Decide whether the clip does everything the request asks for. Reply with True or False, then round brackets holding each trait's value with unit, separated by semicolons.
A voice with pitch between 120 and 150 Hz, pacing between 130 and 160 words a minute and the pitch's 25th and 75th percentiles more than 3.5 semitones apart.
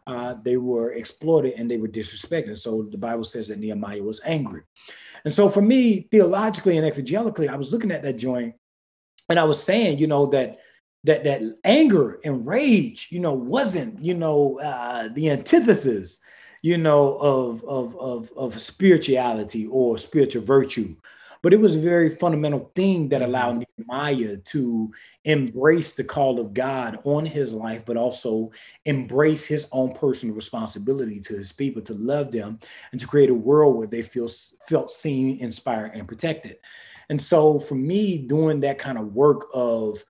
False (135 Hz; 170 wpm; 4.9 semitones)